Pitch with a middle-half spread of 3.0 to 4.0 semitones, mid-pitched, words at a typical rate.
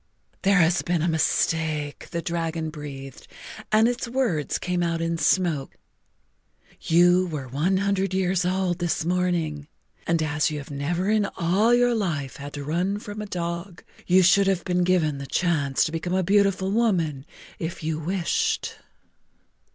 Yes: average, 3.4 semitones; medium, 175 Hz; average, 160 wpm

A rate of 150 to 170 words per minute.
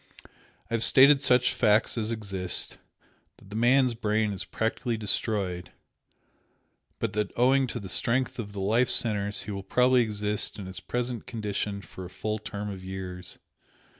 Yes: average, 165 wpm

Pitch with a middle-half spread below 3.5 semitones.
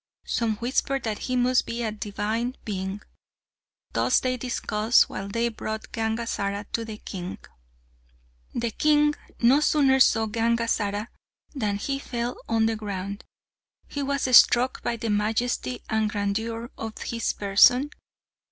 Yes: average, 2.8 semitones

